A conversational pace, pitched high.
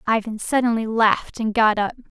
Yes: average, 165 wpm; high, 220 Hz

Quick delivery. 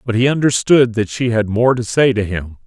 Yes: fast, 250 wpm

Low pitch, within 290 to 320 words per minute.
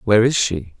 No: low, 105 Hz; fast, 225 wpm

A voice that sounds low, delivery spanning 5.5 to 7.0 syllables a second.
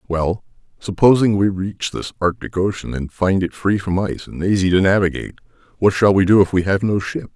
Yes: very low, 95 Hz; 5.6 syllables/s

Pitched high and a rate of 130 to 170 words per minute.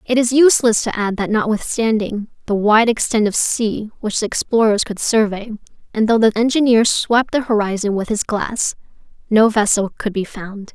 No: high, 220 Hz; average, 180 wpm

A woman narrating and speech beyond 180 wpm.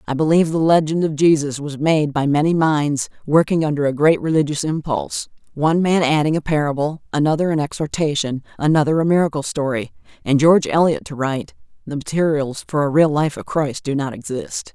No: female; average, 175 wpm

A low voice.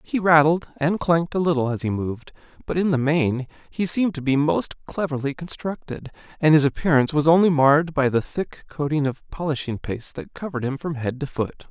No: medium, 150 Hz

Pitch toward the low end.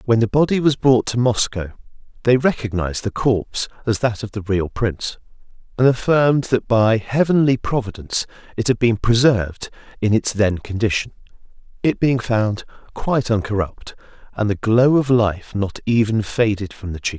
Yes: low, 115 Hz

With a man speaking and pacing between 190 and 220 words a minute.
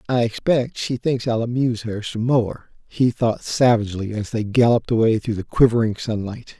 No: male; average, 180 wpm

